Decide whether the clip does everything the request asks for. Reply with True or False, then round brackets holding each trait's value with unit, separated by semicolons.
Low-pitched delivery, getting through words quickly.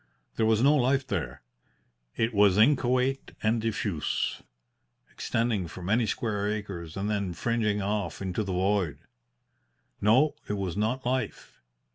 False (105 Hz; 135 wpm)